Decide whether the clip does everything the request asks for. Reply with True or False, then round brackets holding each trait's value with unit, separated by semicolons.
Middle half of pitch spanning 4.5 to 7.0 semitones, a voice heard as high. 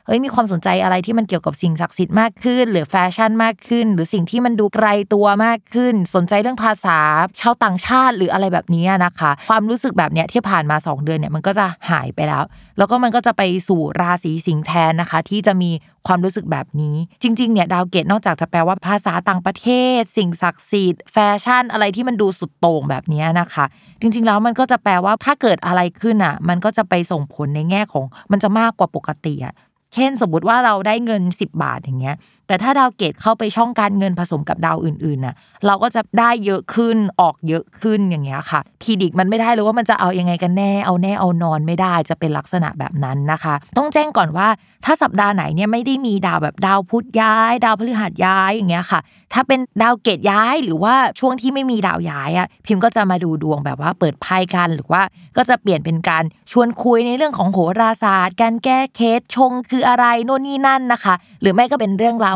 True (4.9 semitones; 195 Hz)